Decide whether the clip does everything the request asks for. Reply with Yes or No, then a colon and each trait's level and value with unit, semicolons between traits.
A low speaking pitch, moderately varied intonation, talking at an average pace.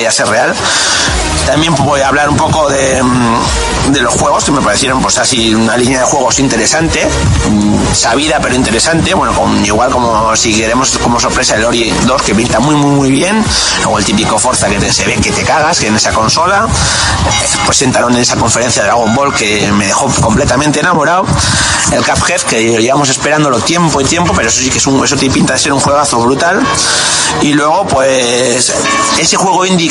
No: low, 130 Hz; average, 3.9 semitones; fast, 200 wpm